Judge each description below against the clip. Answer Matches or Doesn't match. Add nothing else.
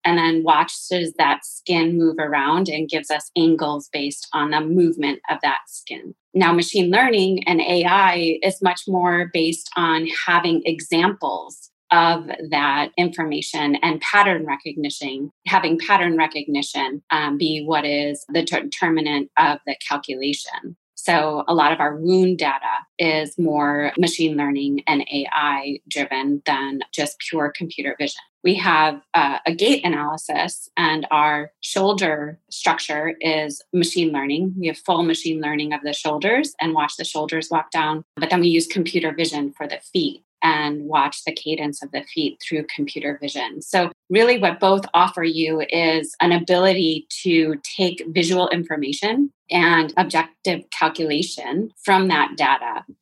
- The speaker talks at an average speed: Matches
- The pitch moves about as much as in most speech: Matches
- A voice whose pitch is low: Doesn't match